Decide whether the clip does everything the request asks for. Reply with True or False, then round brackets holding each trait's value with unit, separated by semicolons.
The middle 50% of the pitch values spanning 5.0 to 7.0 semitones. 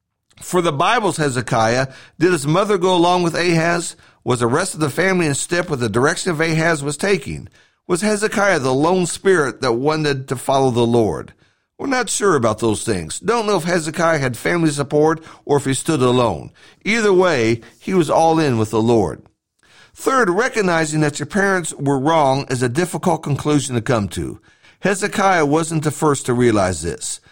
True (5.5 semitones)